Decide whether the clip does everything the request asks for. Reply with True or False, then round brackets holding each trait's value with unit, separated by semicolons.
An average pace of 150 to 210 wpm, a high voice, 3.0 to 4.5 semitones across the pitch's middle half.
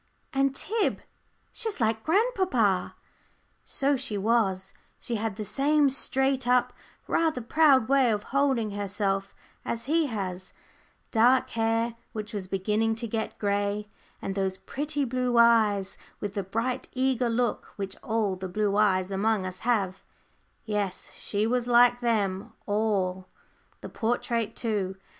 False (140 wpm; 225 Hz; 3.9 semitones)